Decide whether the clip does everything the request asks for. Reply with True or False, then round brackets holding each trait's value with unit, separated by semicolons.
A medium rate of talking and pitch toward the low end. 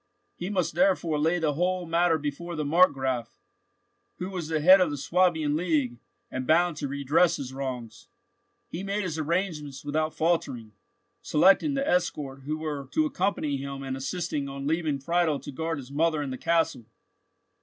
False (170 wpm; 155 Hz)